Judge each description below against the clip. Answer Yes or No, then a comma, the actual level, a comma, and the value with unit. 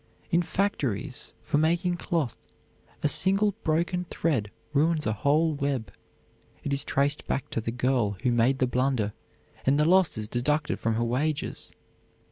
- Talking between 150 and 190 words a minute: Yes, average, 155 wpm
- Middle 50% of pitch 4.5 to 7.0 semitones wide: Yes, average, 5.0 semitones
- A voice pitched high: No, medium, 140 Hz